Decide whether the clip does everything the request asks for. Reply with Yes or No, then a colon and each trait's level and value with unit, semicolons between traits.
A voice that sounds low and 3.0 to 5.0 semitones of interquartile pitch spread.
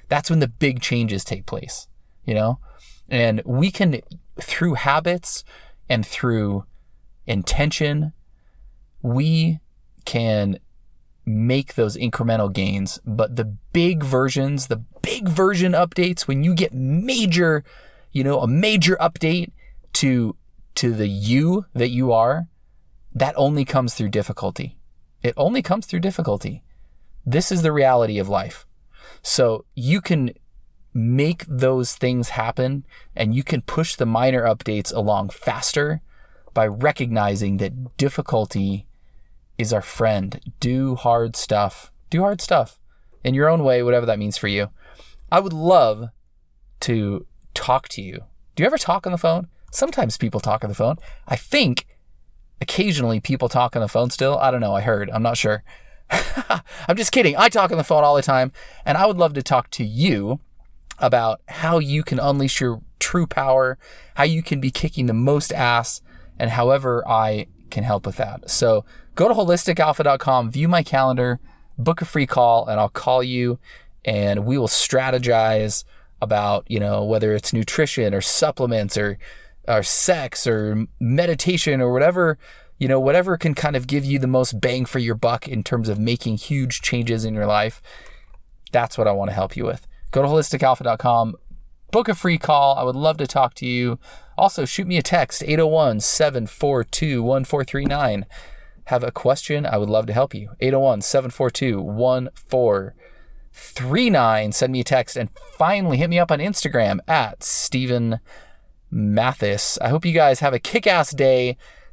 No: low, 130 Hz; wide, 5.6 semitones